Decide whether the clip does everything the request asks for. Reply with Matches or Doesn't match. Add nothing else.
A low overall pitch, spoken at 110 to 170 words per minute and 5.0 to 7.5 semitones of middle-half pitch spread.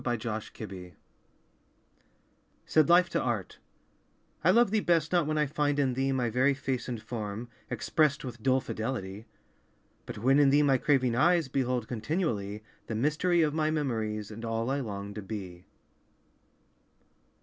Matches